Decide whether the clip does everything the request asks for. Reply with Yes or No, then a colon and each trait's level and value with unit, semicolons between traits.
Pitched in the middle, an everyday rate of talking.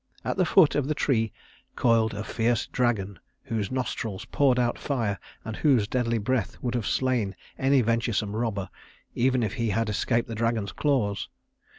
No: low, 115 Hz; average, 170 wpm